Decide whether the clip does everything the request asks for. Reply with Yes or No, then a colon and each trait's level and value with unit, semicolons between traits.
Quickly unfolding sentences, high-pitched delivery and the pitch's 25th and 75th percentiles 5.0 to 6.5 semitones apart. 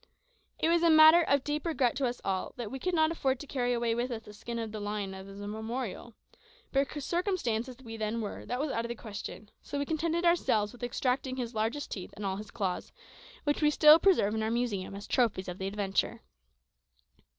Yes: fast, 225 wpm; high, 240 Hz; wide, 5.5 semitones